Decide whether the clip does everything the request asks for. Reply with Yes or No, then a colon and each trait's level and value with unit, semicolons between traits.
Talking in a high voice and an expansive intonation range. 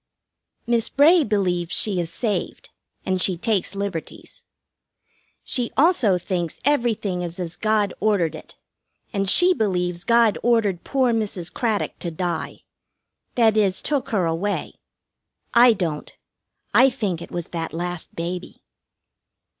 No: high, 200 Hz; average, 4.6 semitones